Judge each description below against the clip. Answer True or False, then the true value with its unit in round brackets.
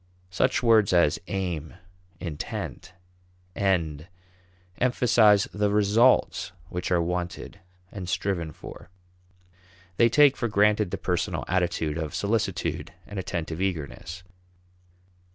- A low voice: True (95 Hz)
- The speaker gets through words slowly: True (105 wpm)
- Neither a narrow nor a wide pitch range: True (3.6 semitones)